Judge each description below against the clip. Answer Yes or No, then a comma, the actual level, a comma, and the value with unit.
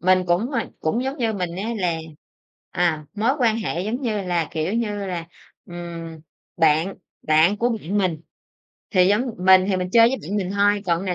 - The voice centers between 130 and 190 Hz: Yes, medium, 185 Hz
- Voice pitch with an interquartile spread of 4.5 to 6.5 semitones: No, average, 3.9 semitones